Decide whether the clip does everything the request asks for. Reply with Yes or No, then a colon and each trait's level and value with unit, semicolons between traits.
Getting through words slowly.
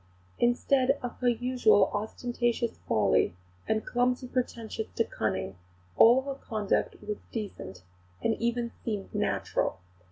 Yes: slow, 120 wpm